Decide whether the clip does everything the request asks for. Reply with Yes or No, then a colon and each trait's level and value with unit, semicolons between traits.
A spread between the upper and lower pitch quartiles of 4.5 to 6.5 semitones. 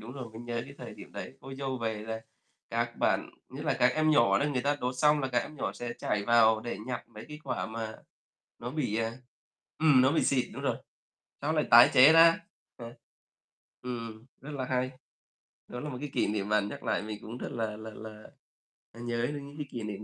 No: average, 3.8 semitones